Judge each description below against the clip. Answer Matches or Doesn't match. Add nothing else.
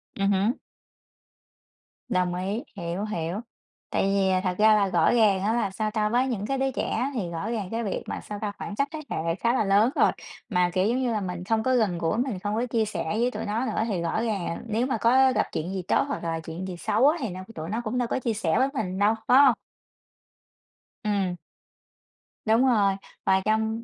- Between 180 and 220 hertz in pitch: Matches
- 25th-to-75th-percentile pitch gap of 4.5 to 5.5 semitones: Doesn't match